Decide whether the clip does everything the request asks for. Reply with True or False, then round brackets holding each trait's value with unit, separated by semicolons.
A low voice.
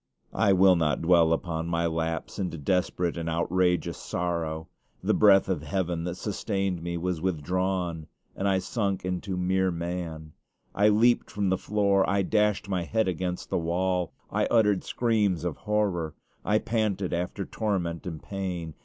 True (90 Hz)